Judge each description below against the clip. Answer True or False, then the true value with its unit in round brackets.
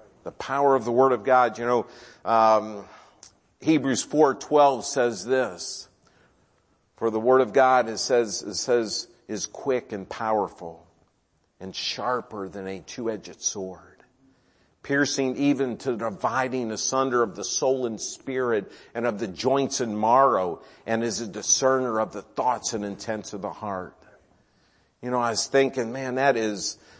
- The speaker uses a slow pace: False (155 wpm)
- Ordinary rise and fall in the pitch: True (3.8 semitones)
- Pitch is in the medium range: False (120 Hz)